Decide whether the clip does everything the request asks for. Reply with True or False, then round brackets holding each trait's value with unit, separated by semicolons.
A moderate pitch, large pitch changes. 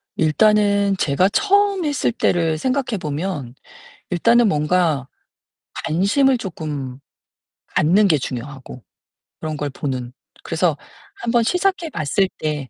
True (180 Hz; 7.7 semitones)